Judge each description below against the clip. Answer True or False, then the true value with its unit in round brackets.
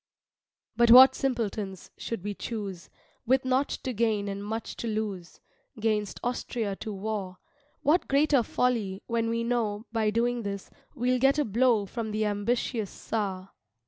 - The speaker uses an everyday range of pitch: True (3.0 semitones)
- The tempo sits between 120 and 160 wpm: True (150 wpm)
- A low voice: False (225 Hz)